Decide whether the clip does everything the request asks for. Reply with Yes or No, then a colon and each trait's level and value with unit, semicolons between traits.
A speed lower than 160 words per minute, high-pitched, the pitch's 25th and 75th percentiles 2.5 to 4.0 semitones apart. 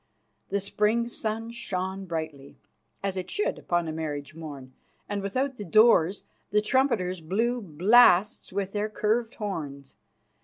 No: average, 140 wpm; high, 195 Hz; average, 5.2 semitones